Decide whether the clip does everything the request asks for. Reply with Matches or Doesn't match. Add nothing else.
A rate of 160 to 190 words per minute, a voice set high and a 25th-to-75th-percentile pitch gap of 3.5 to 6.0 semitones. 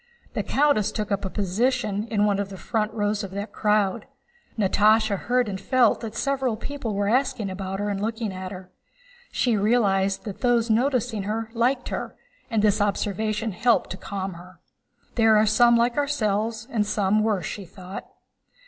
Doesn't match